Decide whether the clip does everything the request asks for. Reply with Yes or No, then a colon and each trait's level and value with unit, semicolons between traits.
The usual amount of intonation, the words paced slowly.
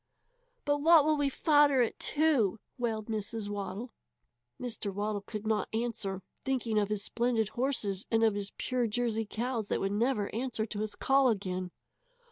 No: average, 3.6 semitones; average, 165 wpm